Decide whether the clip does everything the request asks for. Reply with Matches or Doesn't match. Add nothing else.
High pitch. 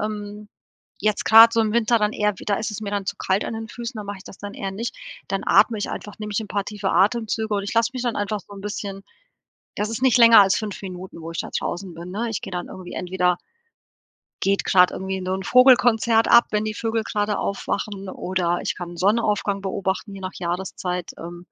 Matches